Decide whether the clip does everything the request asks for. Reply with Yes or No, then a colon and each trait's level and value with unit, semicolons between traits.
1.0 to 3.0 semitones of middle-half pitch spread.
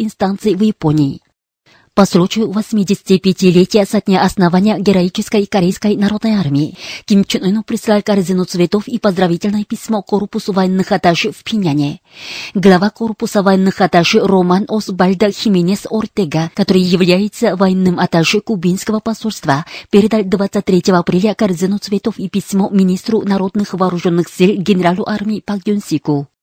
Yes: narrow, 2.5 semitones